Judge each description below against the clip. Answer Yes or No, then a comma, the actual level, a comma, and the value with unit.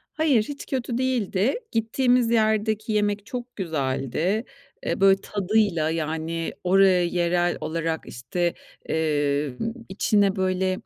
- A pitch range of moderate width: Yes, average, 4.9 semitones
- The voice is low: No, high, 190 Hz